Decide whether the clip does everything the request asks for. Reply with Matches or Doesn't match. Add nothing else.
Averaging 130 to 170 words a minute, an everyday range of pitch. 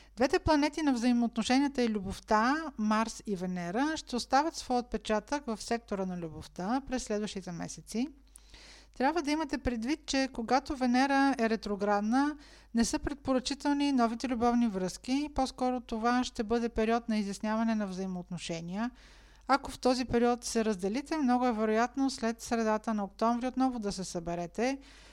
Matches